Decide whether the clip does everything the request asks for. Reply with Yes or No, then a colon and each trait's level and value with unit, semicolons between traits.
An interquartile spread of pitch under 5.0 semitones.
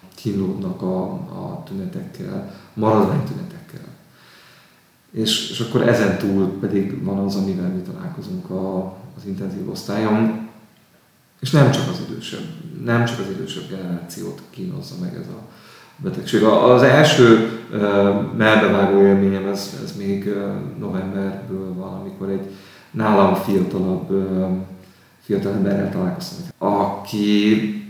No: wide, 7.4 semitones